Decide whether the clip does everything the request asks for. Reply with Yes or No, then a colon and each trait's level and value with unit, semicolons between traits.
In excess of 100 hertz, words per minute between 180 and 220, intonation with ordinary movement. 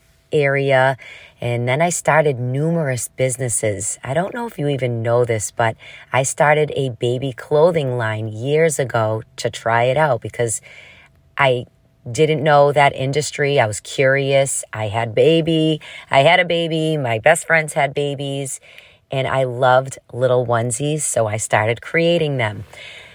No: low, 135 Hz; average, 155 wpm; average, 4.1 semitones